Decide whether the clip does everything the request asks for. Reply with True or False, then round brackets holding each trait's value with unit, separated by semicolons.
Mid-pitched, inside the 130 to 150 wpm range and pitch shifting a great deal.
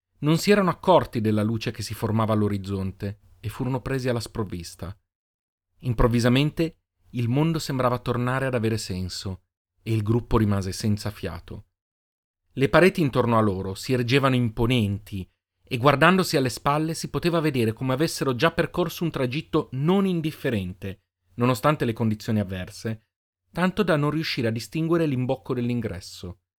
False (120 Hz; 145 wpm; 6.3 semitones)